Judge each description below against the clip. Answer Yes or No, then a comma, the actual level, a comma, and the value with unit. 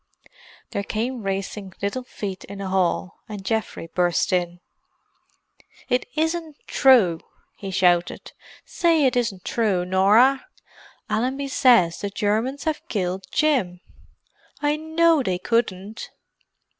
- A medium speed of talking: No, slow, 115 wpm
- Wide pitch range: Yes, wide, 5.8 semitones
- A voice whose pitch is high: Yes, high, 210 Hz